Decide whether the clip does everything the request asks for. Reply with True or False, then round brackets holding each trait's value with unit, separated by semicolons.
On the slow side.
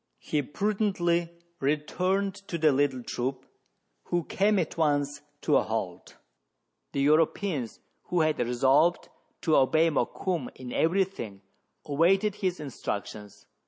True (125 wpm)